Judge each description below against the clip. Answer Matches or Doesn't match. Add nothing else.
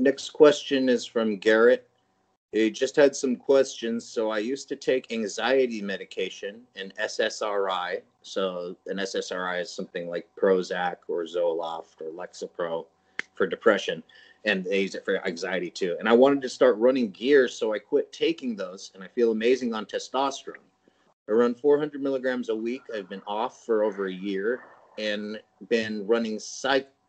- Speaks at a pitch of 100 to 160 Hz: Matches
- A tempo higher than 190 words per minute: Doesn't match